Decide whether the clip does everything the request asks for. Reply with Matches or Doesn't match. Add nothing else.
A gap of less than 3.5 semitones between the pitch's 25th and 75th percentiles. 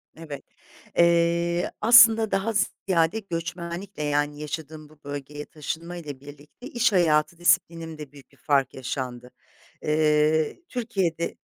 Matches